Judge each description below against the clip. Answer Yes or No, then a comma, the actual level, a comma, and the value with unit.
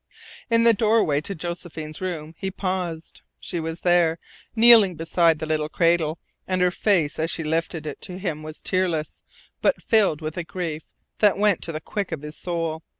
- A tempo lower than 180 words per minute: No, average, 185 wpm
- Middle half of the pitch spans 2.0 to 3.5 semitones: Yes, average, 2.9 semitones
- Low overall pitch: No, medium, 170 Hz